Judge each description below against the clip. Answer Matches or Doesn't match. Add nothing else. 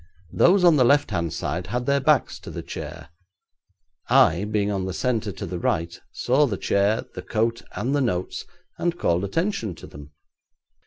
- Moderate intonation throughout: Doesn't match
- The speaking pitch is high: Doesn't match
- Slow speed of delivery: Doesn't match